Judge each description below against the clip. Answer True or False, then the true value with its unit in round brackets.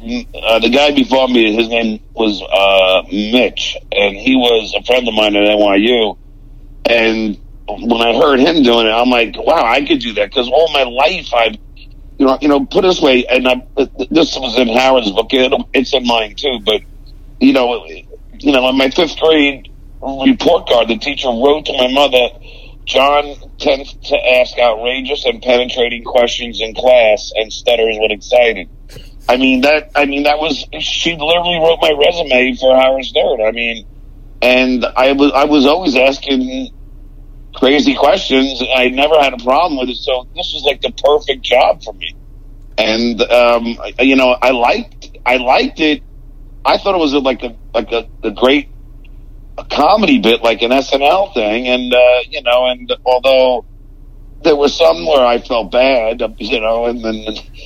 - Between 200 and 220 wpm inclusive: False (180 wpm)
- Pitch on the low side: True (125 Hz)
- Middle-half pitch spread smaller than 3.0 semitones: False (3.4 semitones)